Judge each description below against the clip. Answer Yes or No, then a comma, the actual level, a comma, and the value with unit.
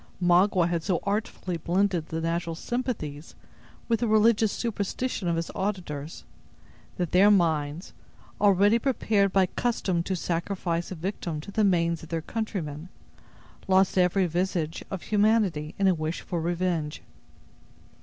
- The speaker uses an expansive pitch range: No, average, 3.4 semitones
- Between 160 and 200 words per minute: No, average, 140 wpm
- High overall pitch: No, medium, 180 Hz